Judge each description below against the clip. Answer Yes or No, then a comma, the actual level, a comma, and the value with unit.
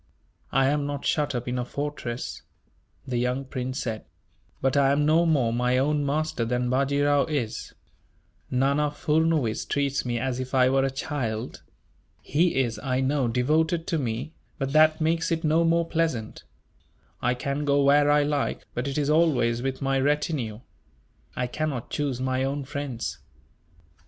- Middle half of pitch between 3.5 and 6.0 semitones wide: No, average, 2.9 semitones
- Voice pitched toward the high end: No, medium, 140 Hz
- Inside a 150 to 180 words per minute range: Yes, average, 165 wpm